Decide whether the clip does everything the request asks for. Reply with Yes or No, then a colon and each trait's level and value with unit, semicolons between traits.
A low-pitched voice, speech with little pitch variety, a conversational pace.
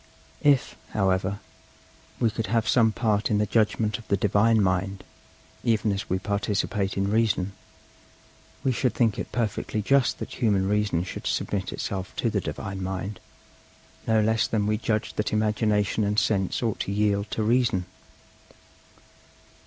Yes: low, 105 Hz; narrow, 2.1 semitones; average, 155 wpm